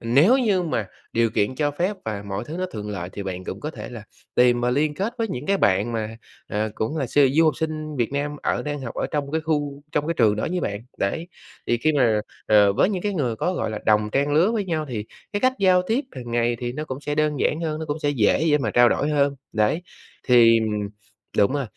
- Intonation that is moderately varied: No, wide, 5.7 semitones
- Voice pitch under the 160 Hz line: Yes, medium, 140 Hz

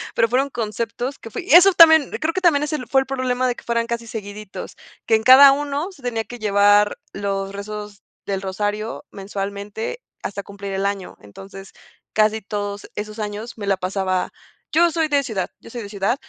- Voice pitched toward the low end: No, high, 215 Hz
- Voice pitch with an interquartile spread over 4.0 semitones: Yes, average, 4.7 semitones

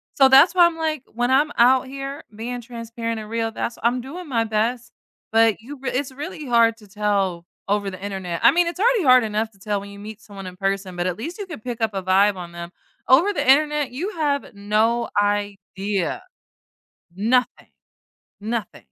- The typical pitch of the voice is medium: No, high, 230 Hz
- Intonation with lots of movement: No, average, 4.8 semitones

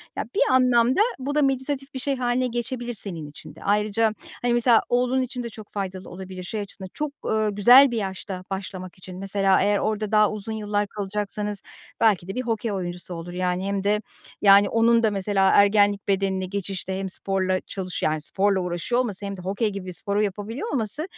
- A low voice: No, high, 205 Hz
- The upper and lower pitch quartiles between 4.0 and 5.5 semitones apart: No, average, 3.5 semitones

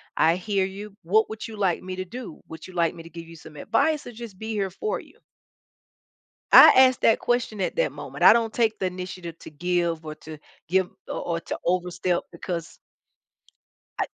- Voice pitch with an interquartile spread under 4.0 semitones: No, average, 4.4 semitones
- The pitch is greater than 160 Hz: Yes, medium, 185 Hz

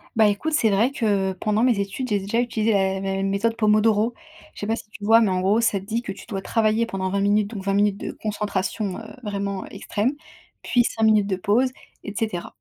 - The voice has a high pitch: Yes, high, 210 Hz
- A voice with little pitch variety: Yes, narrow, 2.3 semitones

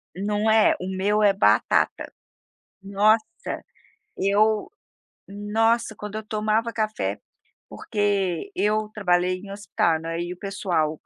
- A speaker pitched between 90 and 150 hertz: No, high, 205 Hz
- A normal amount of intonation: No, narrow, 2.3 semitones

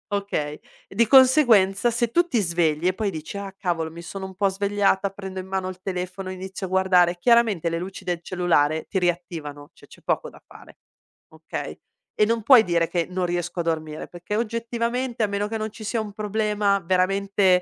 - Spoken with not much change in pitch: No, average, 3.2 semitones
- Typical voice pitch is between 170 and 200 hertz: Yes, high, 190 Hz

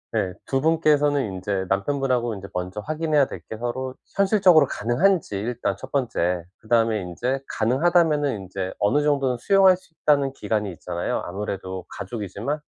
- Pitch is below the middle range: Yes, low, 125 Hz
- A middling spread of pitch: No, wide, 6.9 semitones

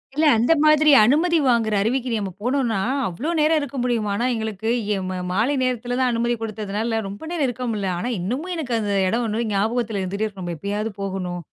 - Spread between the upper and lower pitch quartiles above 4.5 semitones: No, average, 4.0 semitones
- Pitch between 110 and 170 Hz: No, high, 225 Hz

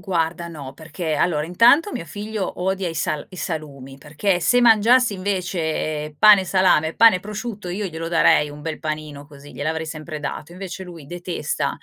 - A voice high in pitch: No, medium, 170 Hz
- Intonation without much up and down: No, average, 4.0 semitones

